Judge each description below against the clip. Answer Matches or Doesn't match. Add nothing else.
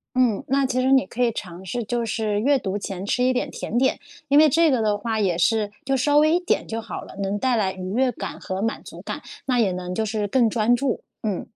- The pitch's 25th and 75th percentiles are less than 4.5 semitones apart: Matches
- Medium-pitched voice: Doesn't match